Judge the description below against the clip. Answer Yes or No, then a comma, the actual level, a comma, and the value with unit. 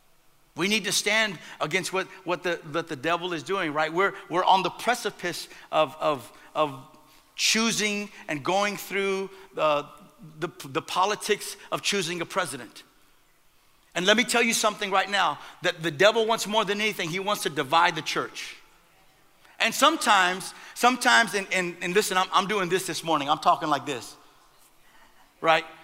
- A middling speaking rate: Yes, average, 170 wpm